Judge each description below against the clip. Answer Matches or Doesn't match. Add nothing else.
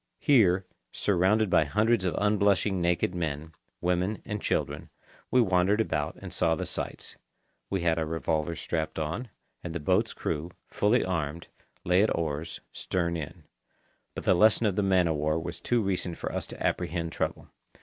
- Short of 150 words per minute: Doesn't match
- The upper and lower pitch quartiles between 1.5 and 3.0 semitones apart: Doesn't match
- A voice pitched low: Matches